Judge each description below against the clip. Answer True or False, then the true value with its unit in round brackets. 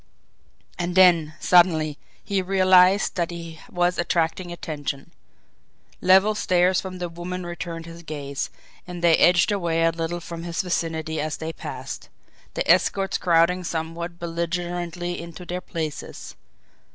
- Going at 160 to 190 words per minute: False (135 wpm)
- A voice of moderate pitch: True (175 Hz)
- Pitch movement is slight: True (1.5 semitones)